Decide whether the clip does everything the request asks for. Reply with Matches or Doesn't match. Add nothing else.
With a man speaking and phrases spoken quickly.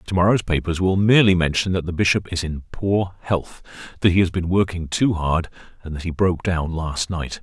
Matches